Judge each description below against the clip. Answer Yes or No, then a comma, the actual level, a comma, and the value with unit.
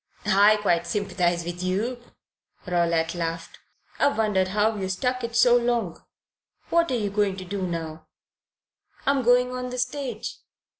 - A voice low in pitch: No, high, 205 Hz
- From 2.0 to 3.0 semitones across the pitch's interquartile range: No, wide, 5.5 semitones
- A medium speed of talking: Yes, average, 150 wpm